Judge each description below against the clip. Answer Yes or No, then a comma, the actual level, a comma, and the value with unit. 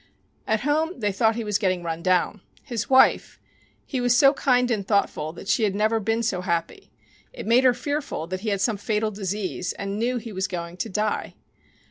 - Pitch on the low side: No, high, 215 Hz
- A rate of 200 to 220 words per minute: Yes, fast, 205 wpm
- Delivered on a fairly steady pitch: No, average, 4.2 semitones